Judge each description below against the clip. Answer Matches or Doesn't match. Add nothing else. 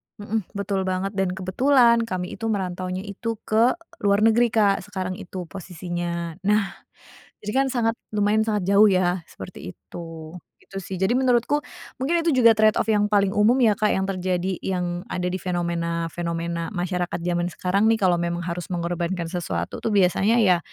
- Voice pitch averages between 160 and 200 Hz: Matches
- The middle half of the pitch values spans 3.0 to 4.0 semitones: Matches